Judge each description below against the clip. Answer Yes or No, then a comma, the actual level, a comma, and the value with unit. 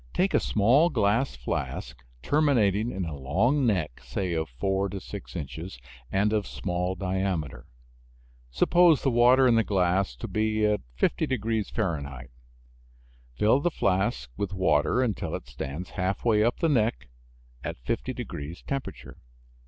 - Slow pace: No, average, 145 wpm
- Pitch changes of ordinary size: No, wide, 5.7 semitones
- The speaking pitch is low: Yes, low, 100 Hz